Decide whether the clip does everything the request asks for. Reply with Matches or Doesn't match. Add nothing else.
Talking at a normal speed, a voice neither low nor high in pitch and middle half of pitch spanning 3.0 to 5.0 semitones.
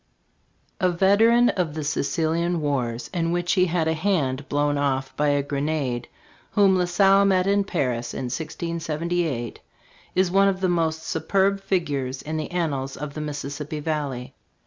Matches